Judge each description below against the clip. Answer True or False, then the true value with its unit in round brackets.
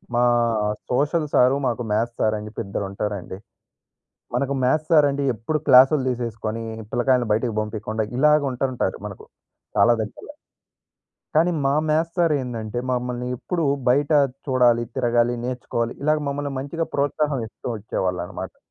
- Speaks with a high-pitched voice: False (125 Hz)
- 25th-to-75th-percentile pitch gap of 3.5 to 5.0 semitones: True (4.0 semitones)